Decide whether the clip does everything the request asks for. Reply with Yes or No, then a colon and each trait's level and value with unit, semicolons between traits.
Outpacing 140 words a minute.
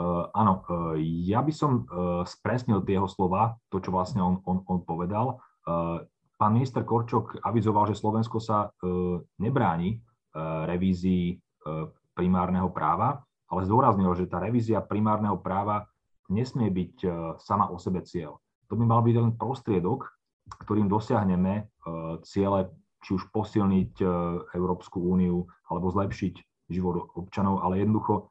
No: average, 125 wpm